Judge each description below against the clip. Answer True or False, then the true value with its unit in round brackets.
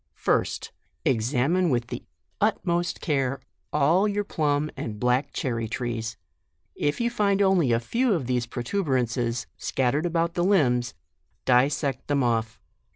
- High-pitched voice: False (135 Hz)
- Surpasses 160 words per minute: False (140 wpm)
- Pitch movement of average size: False (6.1 semitones)